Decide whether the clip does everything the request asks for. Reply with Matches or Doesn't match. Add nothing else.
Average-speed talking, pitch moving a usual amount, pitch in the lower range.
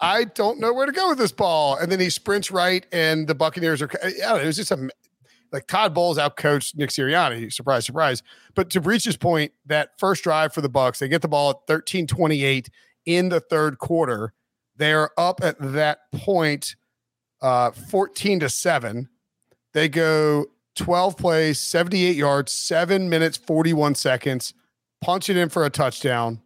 Doesn't match